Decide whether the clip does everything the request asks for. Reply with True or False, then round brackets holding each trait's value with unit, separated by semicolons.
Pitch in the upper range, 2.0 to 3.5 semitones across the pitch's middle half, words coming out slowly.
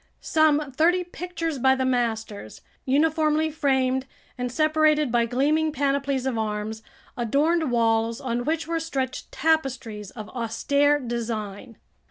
False (265 Hz; 4.9 semitones; 125 wpm)